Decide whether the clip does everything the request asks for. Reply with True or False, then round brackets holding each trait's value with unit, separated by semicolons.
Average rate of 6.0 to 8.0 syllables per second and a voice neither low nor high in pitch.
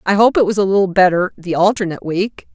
False (6.4 syllables/s; 195 Hz)